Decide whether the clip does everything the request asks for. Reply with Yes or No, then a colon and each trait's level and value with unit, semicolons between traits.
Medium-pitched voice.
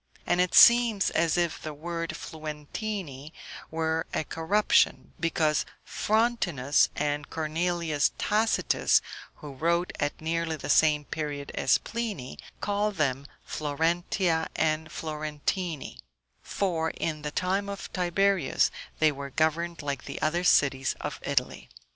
Yes: medium, 160 Hz